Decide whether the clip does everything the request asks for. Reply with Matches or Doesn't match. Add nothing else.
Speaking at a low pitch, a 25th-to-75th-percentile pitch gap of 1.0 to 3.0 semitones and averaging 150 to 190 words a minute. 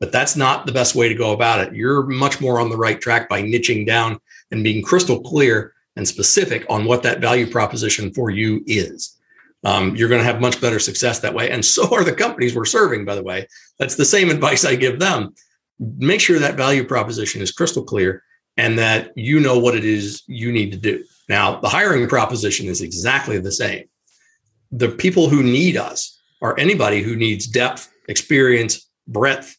Doesn't match